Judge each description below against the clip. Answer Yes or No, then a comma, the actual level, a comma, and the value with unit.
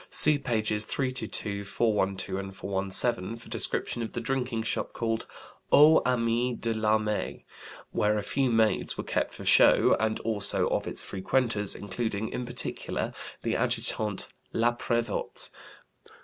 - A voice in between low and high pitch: No, low, 110 Hz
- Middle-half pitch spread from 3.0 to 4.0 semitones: No, narrow, 2.5 semitones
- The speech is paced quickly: No, slow, 135 wpm